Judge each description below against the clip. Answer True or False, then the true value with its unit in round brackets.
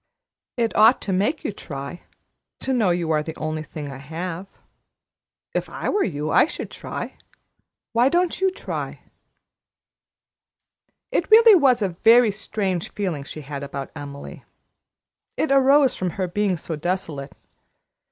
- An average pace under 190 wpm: True (145 wpm)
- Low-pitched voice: False (185 Hz)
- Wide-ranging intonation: True (7.7 semitones)